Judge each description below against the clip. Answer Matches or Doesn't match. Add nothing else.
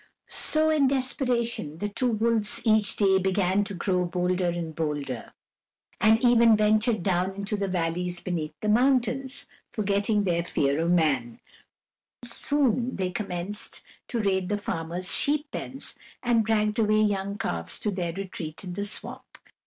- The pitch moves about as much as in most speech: Matches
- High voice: Matches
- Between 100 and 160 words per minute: Matches